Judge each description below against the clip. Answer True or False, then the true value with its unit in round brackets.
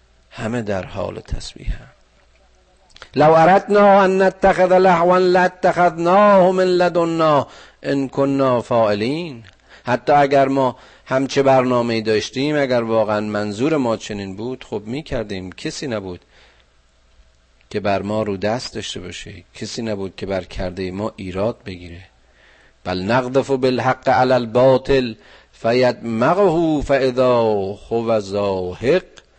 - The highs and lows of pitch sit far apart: True (5.9 semitones)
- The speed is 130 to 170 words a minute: False (120 wpm)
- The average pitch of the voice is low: True (120 Hz)